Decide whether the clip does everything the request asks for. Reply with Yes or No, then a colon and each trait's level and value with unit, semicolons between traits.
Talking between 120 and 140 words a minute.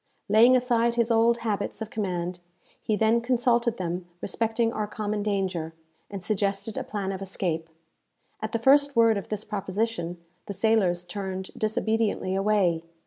No: average, 150 wpm